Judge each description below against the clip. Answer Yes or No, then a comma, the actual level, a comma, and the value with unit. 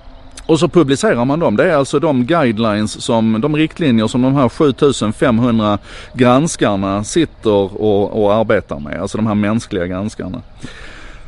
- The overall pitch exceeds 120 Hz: No, low, 115 Hz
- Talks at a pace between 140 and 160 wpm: Yes, average, 150 wpm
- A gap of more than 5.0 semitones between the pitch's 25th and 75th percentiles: Yes, wide, 5.4 semitones